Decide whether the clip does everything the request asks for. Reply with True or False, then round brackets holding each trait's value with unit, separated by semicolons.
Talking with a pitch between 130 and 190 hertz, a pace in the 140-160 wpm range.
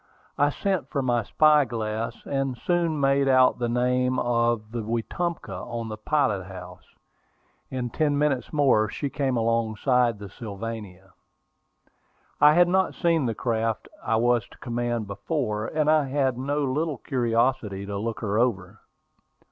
False (120 Hz; 150 wpm)